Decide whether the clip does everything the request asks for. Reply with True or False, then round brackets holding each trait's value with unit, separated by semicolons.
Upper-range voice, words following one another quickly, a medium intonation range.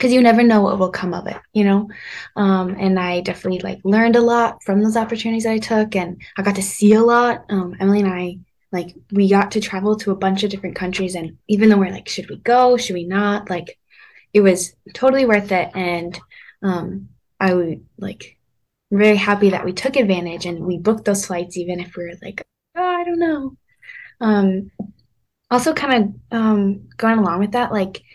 True (200 Hz; 210 wpm; 3.5 semitones)